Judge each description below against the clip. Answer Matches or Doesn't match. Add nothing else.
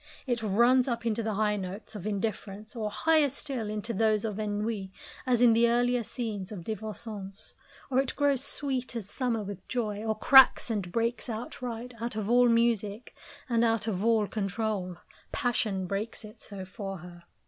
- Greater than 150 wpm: Matches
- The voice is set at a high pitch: Matches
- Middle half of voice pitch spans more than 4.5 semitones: Doesn't match